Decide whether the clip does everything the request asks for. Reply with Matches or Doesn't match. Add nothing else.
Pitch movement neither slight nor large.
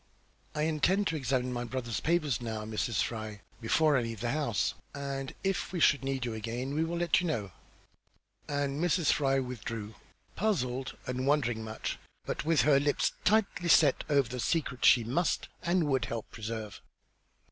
Matches